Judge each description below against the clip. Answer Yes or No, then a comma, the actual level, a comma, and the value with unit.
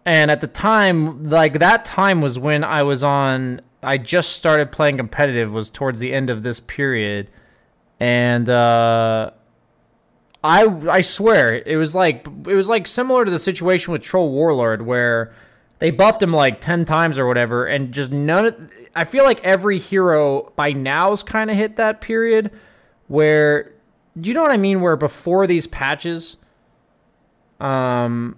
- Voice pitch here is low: No, medium, 155 Hz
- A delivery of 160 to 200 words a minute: Yes, average, 165 wpm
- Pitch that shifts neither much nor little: No, wide, 6.6 semitones